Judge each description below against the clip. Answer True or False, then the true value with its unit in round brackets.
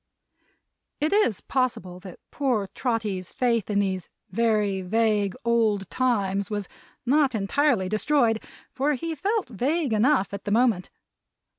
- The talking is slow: True (130 wpm)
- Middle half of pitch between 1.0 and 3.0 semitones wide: False (4.6 semitones)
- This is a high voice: True (225 Hz)